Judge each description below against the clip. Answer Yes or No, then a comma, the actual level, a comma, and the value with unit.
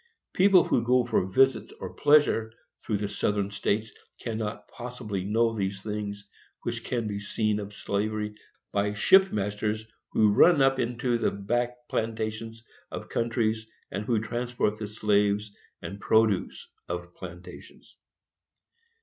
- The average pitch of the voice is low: Yes, low, 110 Hz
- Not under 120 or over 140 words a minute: Yes, slow, 135 wpm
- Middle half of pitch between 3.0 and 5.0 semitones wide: No, narrow, 2.5 semitones